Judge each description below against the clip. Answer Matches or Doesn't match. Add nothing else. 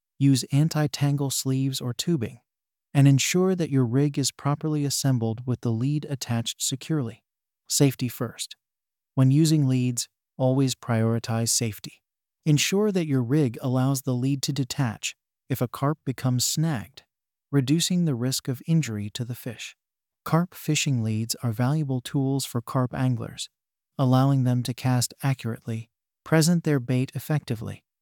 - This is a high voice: Doesn't match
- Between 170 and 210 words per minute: Doesn't match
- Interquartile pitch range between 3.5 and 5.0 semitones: Doesn't match